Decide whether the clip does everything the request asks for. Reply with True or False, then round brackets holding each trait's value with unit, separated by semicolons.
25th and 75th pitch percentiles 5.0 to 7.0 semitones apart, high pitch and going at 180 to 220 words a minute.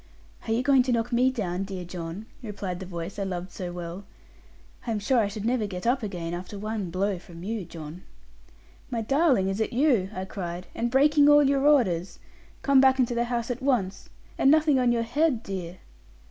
True (5.6 semitones; 215 Hz; 205 wpm)